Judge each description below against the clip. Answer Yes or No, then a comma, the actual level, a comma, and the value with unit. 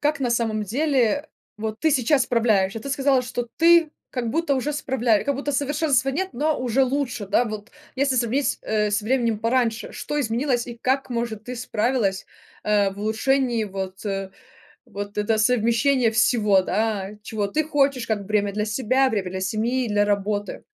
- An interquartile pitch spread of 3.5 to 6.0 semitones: Yes, average, 4.1 semitones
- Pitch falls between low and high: No, high, 235 Hz